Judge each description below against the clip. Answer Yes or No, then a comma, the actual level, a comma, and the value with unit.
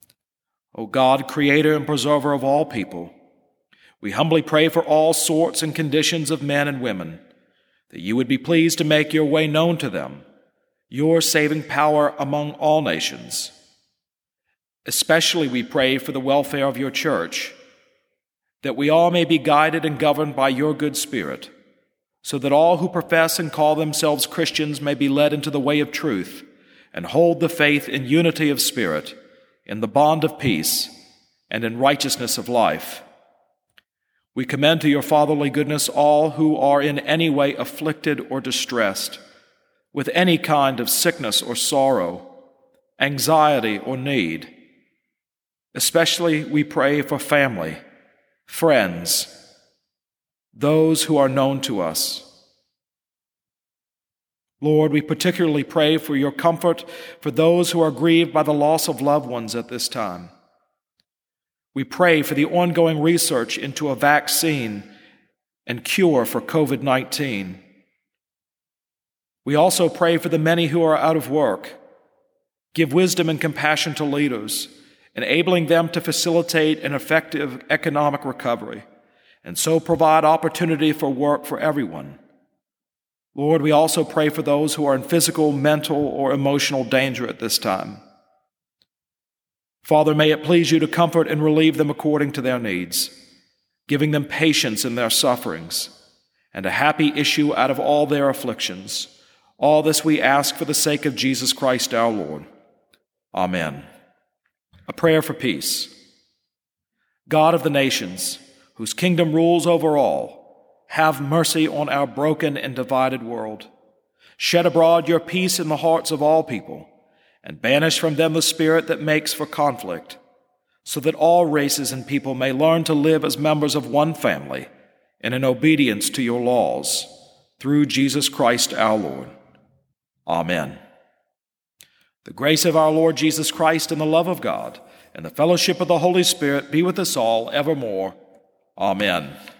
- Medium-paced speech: Yes, average, 150 wpm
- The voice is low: No, medium, 150 Hz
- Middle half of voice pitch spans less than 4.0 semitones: Yes, narrow, 2.6 semitones